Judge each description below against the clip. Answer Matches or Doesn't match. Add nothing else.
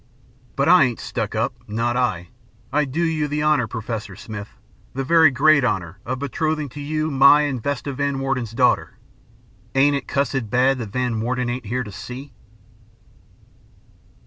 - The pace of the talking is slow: Doesn't match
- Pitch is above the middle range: Doesn't match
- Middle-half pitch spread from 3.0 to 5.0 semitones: Matches